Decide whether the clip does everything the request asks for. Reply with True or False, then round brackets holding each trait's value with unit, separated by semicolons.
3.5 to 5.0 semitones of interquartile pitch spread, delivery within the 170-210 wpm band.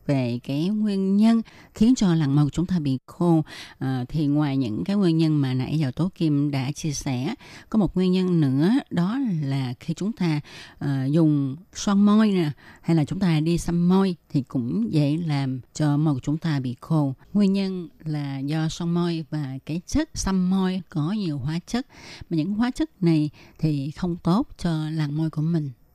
True (4.2 semitones; 205 wpm)